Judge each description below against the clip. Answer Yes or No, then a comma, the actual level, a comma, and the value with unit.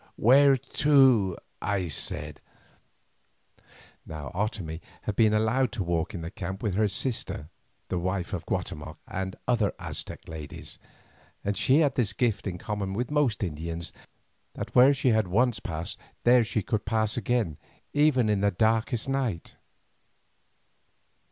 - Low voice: Yes, low, 105 Hz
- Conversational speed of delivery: Yes, average, 145 wpm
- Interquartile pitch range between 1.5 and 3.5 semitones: No, average, 5.0 semitones